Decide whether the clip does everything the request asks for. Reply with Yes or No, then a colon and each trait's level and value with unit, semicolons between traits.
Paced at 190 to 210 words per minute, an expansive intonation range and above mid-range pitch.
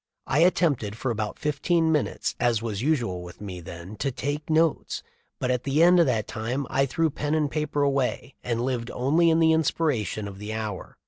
No: average, 200 wpm; wide, 5.9 semitones; low, 135 Hz